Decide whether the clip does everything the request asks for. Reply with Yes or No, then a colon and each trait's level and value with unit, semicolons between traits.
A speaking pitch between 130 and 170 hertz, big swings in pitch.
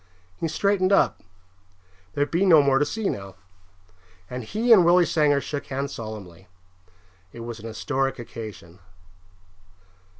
Yes: medium, 140 Hz; wide, 7.3 semitones